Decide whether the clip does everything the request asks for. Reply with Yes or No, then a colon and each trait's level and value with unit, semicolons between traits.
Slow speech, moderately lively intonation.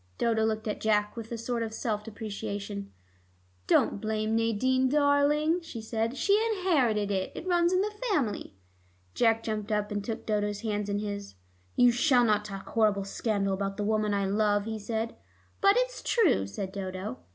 No: average, 175 wpm; average, 3.2 semitones